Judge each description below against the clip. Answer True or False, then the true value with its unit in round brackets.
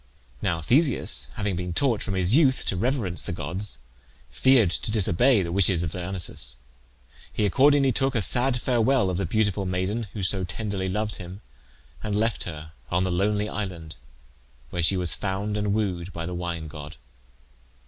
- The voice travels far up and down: False (3.8 semitones)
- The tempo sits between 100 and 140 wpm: False (170 wpm)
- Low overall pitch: True (95 Hz)